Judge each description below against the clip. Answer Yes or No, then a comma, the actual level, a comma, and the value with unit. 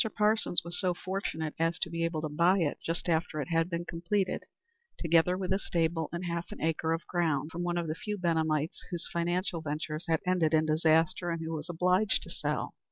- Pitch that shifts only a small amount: Yes, narrow, 1.7 semitones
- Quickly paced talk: Yes, fast, 215 wpm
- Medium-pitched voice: Yes, medium, 170 Hz